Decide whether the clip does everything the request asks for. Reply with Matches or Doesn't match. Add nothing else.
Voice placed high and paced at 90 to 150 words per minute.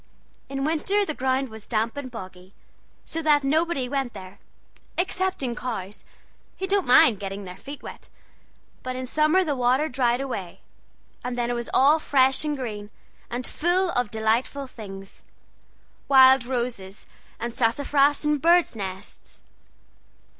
Matches